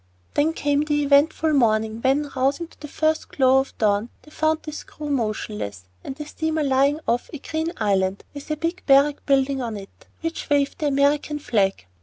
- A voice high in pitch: Yes, very high, 280 Hz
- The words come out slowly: No, average, 195 wpm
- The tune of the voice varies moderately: Yes, average, 4.2 semitones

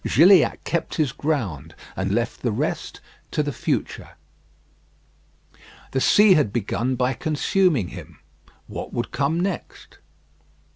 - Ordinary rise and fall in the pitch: No, wide, 7.4 semitones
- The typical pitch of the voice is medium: No, low, 130 Hz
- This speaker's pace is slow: Yes, slow, 125 wpm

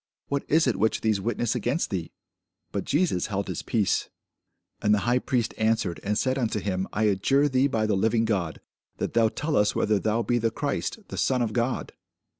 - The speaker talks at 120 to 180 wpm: No, fast, 205 wpm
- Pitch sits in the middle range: No, low, 110 Hz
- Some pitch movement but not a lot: Yes, average, 3.5 semitones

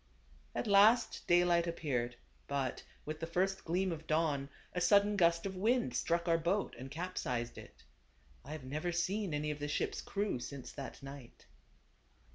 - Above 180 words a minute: No, average, 165 wpm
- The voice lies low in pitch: No, medium, 165 Hz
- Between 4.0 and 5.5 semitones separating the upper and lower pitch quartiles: Yes, average, 4.6 semitones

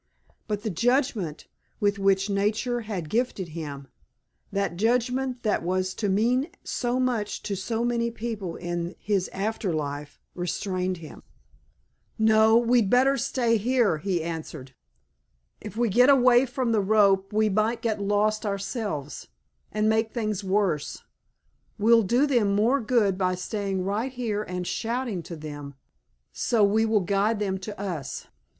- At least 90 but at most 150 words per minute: Yes, average, 145 wpm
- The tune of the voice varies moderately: Yes, average, 3.9 semitones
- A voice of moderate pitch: No, high, 210 Hz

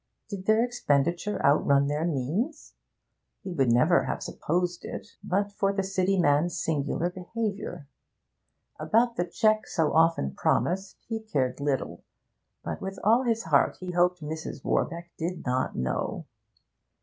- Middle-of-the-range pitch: Yes, medium, 175 Hz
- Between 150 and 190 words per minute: No, average, 140 wpm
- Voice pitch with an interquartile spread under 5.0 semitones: No, average, 5.3 semitones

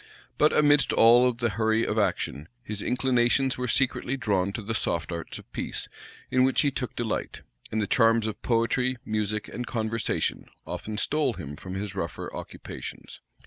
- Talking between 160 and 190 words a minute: Yes, average, 170 wpm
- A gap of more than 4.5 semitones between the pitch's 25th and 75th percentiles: No, average, 3.3 semitones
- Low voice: Yes, low, 115 Hz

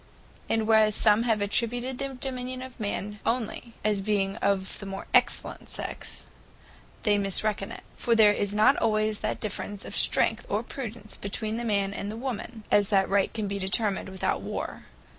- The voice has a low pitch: No, high, 215 Hz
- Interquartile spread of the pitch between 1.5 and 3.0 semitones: Yes, narrow, 2.5 semitones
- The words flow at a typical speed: Yes, average, 190 wpm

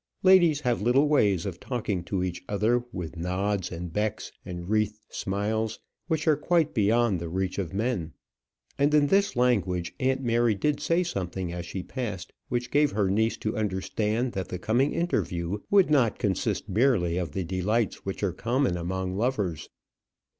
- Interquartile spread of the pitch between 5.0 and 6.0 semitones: Yes, average, 5.3 semitones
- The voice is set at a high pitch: No, low, 105 Hz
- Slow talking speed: No, average, 170 wpm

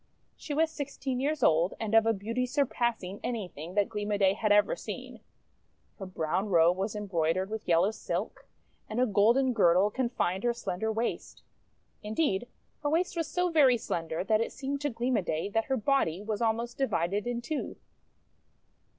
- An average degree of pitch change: Yes, average, 4.9 semitones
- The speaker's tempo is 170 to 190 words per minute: Yes, average, 180 wpm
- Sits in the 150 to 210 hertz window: No, high, 220 Hz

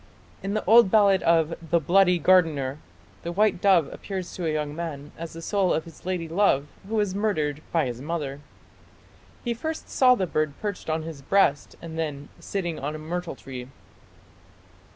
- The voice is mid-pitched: Yes, medium, 170 Hz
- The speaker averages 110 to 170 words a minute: No, average, 180 wpm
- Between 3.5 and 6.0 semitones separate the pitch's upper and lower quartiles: Yes, average, 4.3 semitones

